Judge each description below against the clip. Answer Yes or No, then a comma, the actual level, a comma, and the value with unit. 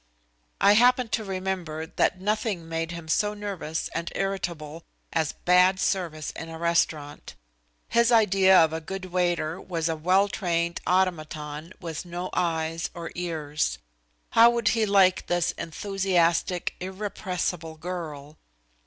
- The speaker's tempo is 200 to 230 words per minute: No, slow, 135 wpm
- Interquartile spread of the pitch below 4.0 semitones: Yes, average, 2.9 semitones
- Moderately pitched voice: Yes, medium, 175 Hz